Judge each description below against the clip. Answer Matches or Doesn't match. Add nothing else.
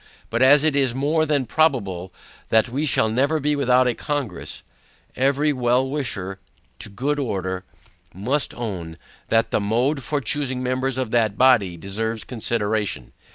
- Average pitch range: Matches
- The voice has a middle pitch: Doesn't match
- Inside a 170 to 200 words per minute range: Doesn't match